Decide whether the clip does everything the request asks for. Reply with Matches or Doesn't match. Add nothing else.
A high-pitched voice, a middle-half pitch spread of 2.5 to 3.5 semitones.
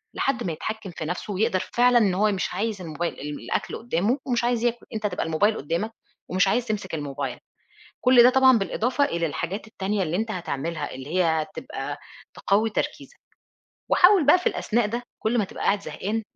Doesn't match